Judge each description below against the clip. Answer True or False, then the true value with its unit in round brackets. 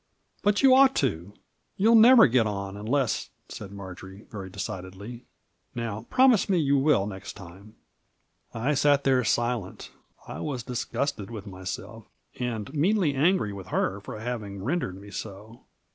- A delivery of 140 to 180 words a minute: True (145 wpm)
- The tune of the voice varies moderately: False (6.2 semitones)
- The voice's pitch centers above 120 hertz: False (115 Hz)